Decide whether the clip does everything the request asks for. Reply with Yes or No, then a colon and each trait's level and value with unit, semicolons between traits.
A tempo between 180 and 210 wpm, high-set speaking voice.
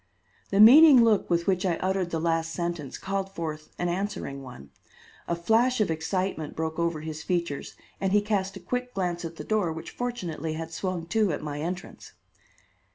No: average, 185 wpm; medium, 175 Hz